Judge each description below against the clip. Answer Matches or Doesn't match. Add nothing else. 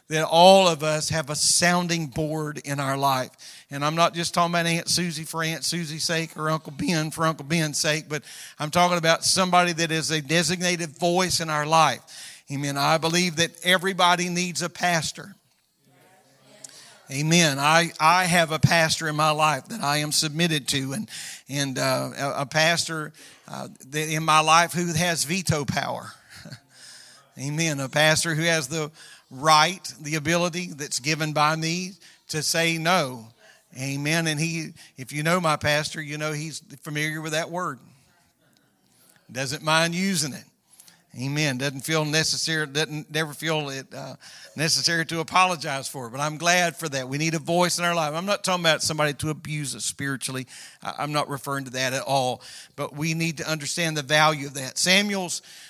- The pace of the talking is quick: Doesn't match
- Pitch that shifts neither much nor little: Doesn't match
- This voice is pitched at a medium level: Matches